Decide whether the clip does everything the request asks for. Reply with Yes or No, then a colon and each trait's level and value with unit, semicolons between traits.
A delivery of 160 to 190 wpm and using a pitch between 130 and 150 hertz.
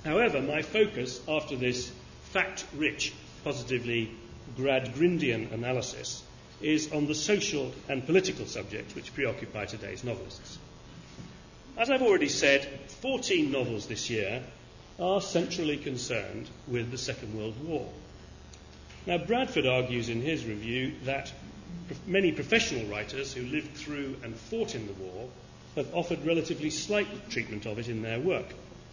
No: slow, 135 wpm; low, 135 Hz